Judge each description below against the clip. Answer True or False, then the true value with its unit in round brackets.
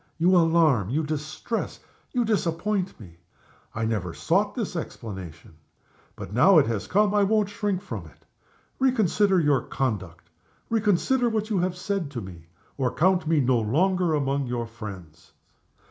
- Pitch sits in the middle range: True (160 Hz)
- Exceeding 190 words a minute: False (155 wpm)